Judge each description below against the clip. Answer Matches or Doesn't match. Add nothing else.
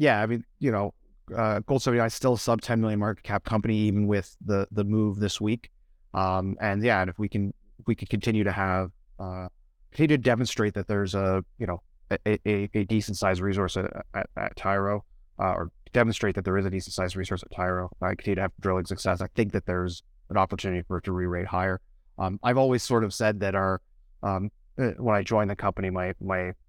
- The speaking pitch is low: Matches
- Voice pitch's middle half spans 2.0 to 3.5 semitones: Matches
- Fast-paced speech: Matches